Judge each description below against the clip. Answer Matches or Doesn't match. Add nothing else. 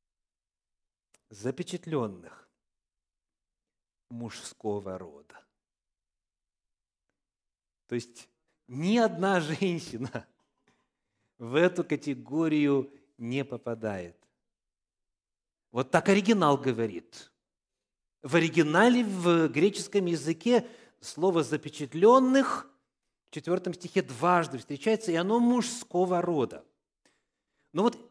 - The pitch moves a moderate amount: Doesn't match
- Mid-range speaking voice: Matches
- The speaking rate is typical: Doesn't match